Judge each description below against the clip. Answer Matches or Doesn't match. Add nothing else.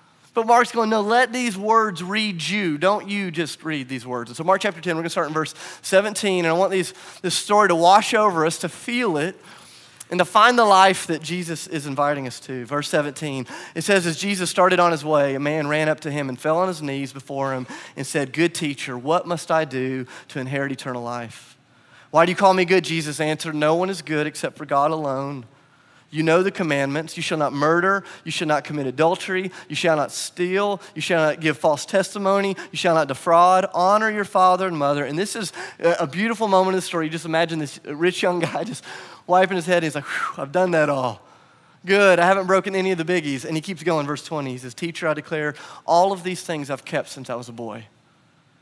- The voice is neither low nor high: Matches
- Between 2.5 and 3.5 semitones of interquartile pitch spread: Doesn't match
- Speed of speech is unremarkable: Doesn't match